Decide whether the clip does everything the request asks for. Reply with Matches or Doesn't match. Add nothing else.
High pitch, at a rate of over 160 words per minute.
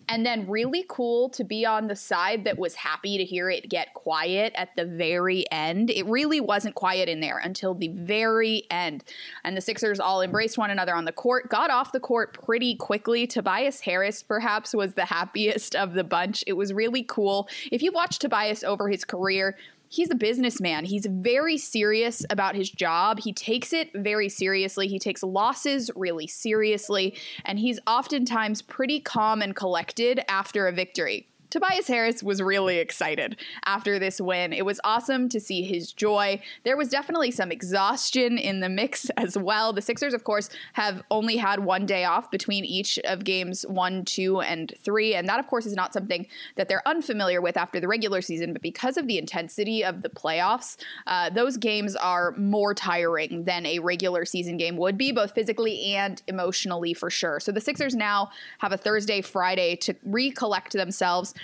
Matches